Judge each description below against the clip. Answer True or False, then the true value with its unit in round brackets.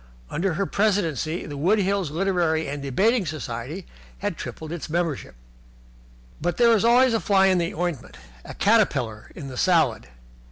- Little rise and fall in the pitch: False (4.8 semitones)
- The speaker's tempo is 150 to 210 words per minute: True (160 wpm)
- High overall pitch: False (175 Hz)